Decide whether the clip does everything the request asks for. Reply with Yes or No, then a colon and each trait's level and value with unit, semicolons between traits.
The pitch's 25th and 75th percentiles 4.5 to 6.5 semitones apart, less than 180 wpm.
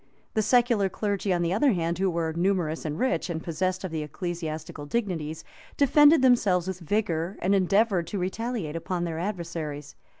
No: average, 3.8 semitones; average, 170 wpm